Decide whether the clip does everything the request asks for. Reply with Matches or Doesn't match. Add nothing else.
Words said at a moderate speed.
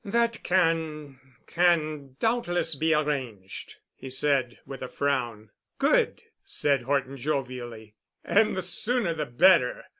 Doesn't match